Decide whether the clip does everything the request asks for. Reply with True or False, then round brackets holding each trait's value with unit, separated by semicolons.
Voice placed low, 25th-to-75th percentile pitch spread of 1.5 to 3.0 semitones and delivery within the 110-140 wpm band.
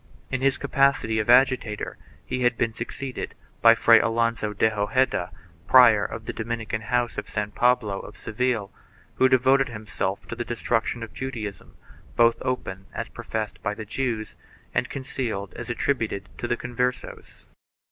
False (115 Hz; 2.7 semitones; 155 wpm)